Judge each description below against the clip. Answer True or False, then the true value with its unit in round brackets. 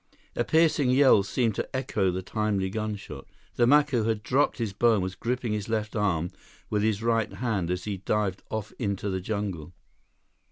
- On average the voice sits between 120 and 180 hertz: False (105 Hz)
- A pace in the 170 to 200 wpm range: True (185 wpm)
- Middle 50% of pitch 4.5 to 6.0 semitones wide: False (3.3 semitones)